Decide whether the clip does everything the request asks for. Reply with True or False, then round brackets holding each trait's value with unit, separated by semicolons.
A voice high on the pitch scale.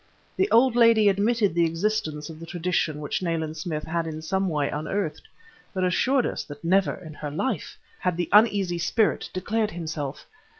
False (175 Hz)